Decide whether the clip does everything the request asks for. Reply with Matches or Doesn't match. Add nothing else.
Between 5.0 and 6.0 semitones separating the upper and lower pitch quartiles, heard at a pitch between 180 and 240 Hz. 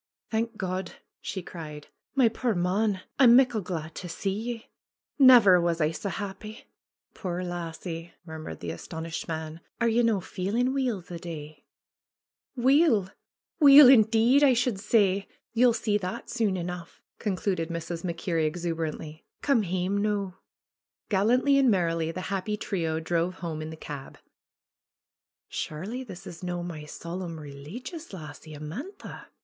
Matches